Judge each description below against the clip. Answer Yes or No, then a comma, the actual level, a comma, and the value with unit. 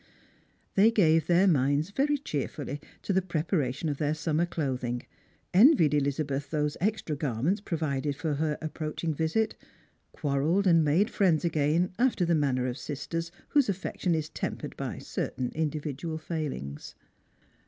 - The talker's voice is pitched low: No, medium, 155 Hz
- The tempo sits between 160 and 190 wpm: No, average, 145 wpm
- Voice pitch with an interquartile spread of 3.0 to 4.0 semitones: Yes, average, 3.5 semitones